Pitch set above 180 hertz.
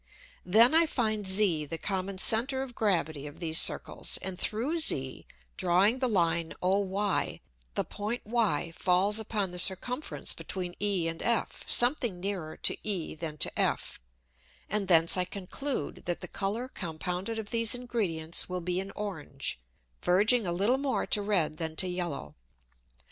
Yes: high, 190 Hz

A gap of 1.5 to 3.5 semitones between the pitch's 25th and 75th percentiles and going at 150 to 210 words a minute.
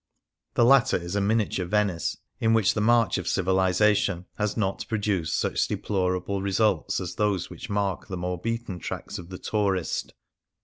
Yes: average, 2.7 semitones; average, 165 wpm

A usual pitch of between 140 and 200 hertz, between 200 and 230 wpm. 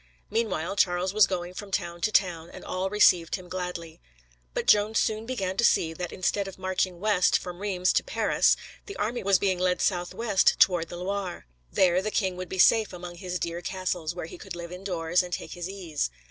Yes: medium, 185 Hz; fast, 205 wpm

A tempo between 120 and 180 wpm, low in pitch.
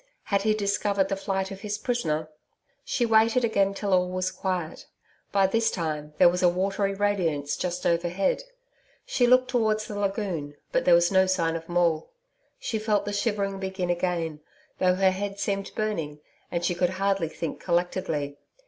No: average, 175 wpm; high, 190 Hz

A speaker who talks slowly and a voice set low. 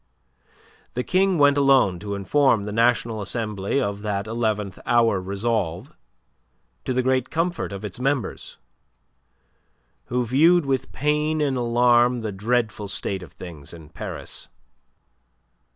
Yes: slow, 130 wpm; low, 120 Hz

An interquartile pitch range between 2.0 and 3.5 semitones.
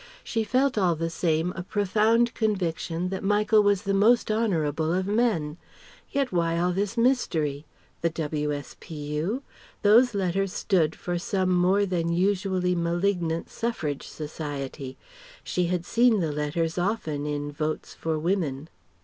No: average, 4.4 semitones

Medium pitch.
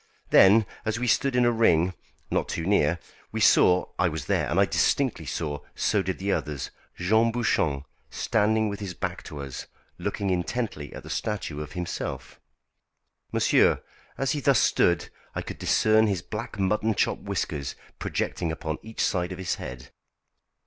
No: very low, 95 Hz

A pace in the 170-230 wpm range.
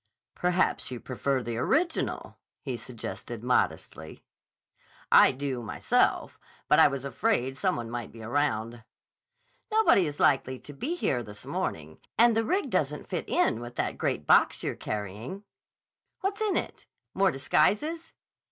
No: average, 145 wpm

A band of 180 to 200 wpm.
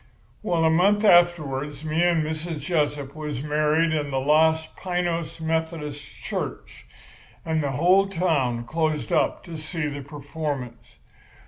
No: slow, 135 wpm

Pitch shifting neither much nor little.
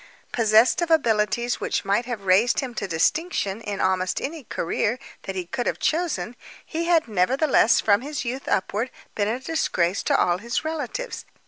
No: wide, 6.1 semitones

